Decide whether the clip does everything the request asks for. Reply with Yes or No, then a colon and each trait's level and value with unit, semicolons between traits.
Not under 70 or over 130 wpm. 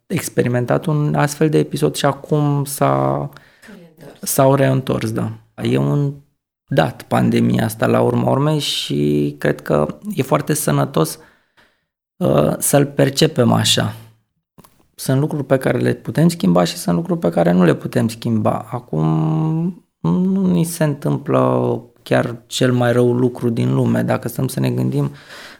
No: average, 145 wpm